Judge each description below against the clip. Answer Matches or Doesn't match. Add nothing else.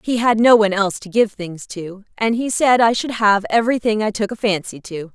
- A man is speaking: Doesn't match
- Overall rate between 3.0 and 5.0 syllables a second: Doesn't match